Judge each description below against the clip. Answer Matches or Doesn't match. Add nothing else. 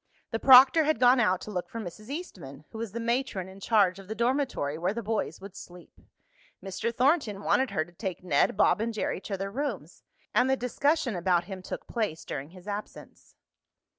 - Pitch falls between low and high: Doesn't match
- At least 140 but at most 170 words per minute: Doesn't match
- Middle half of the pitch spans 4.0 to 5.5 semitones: Matches